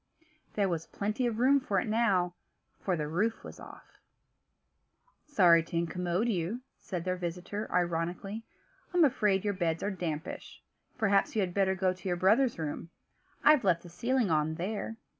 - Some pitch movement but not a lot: Yes, average, 4.0 semitones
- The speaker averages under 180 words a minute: Yes, average, 165 wpm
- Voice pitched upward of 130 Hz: Yes, high, 190 Hz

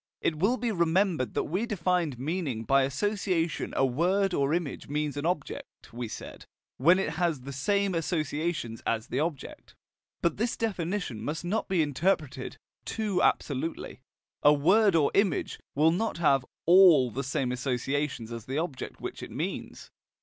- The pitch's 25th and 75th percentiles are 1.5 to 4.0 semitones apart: No, average, 5.3 semitones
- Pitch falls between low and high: Yes, medium, 160 Hz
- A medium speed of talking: Yes, average, 160 wpm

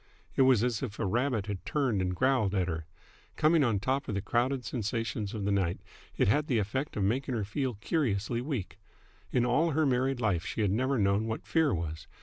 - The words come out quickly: Yes, fast, 215 wpm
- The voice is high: No, low, 115 Hz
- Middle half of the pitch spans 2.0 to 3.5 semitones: No, average, 4.9 semitones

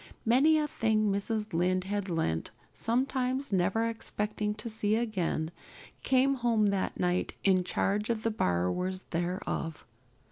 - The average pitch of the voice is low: No, high, 210 Hz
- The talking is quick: No, average, 140 wpm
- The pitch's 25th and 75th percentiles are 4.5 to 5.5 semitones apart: No, average, 3.9 semitones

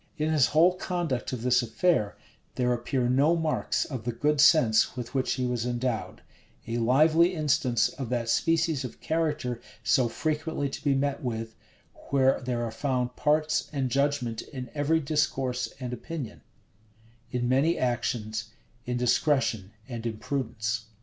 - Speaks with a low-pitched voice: Yes, low, 130 Hz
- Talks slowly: No, average, 150 wpm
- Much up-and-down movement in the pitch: No, average, 3.9 semitones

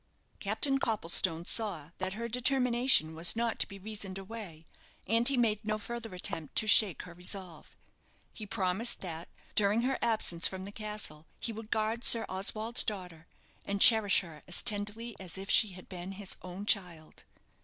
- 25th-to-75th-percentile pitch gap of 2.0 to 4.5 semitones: Yes, average, 3.7 semitones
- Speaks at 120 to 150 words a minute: No, average, 170 wpm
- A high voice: Yes, high, 205 Hz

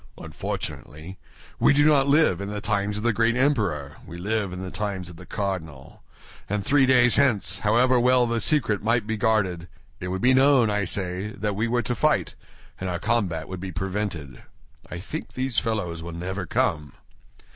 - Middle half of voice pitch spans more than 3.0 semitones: Yes, average, 4.6 semitones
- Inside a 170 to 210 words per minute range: Yes, average, 190 wpm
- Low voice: Yes, low, 105 Hz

